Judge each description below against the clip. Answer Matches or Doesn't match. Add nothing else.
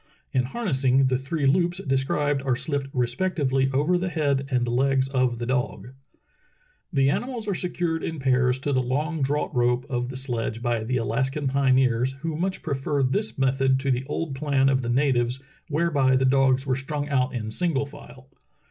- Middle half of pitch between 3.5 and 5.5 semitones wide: Doesn't match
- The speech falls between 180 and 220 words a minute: Matches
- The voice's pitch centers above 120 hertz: Matches